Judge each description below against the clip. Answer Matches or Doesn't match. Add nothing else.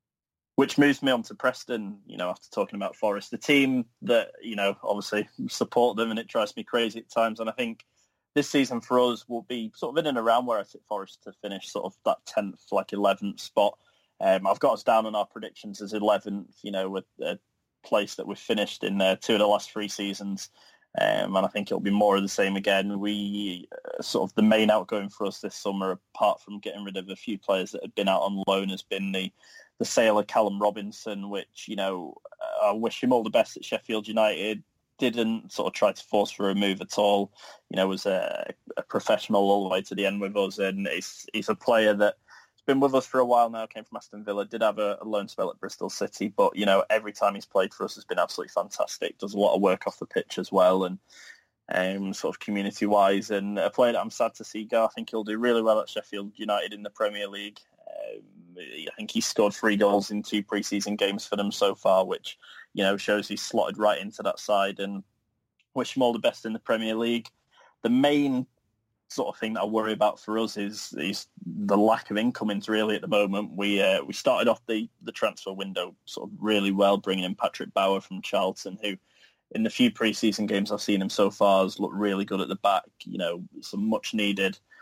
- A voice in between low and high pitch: Doesn't match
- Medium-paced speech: Doesn't match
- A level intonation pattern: Matches